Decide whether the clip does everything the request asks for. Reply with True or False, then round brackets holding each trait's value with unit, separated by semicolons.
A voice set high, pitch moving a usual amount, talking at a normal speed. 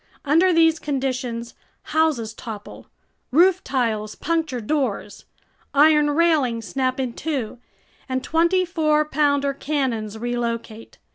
False (275 Hz; 5.0 semitones; 110 wpm)